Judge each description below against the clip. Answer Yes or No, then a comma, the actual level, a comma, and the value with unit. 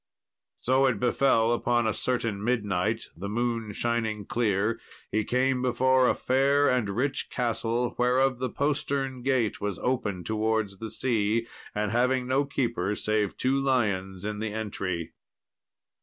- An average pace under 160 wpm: Yes, average, 140 wpm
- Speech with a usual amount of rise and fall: Yes, average, 3.5 semitones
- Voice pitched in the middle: No, low, 115 Hz